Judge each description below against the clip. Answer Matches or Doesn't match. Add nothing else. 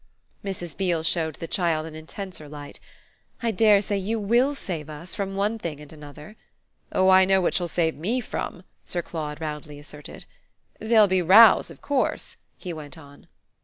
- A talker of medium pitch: Matches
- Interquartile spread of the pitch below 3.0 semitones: Doesn't match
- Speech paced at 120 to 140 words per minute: Doesn't match